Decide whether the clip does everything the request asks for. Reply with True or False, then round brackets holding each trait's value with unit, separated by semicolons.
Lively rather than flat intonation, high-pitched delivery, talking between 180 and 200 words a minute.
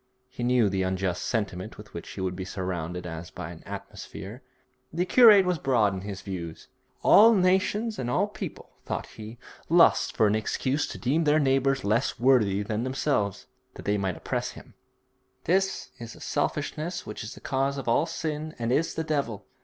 False (7.6 semitones; 120 Hz; 185 wpm)